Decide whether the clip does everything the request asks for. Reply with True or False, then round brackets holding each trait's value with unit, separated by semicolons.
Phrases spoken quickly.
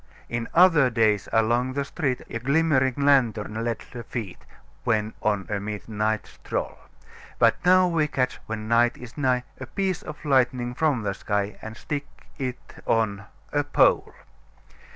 False (150 wpm)